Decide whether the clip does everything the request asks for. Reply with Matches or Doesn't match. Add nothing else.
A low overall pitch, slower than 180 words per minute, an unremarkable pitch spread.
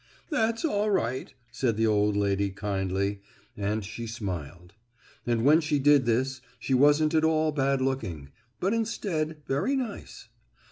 Doesn't match